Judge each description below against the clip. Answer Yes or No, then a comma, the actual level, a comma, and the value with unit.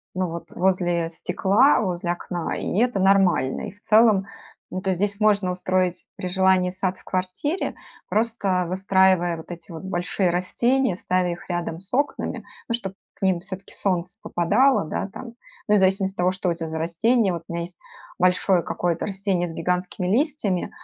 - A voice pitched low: No, medium, 185 Hz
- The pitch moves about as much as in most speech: No, narrow, 2.2 semitones